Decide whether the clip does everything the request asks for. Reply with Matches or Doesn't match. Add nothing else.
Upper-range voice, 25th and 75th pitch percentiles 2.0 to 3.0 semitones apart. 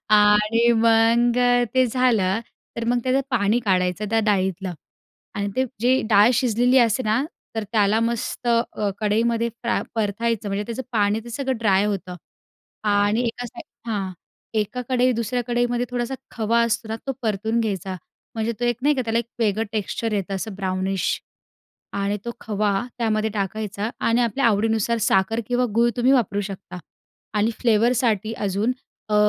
Matches